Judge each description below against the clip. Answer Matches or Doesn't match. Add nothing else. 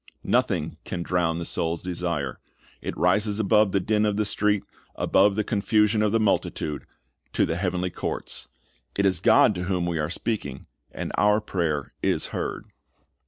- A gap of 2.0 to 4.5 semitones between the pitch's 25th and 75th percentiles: Matches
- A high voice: Doesn't match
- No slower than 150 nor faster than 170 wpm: Matches